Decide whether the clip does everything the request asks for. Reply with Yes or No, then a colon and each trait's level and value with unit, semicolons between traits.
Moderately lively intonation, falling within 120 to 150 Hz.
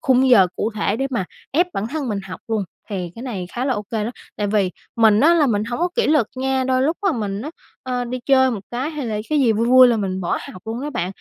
No: average, 4.2 semitones; high, 240 Hz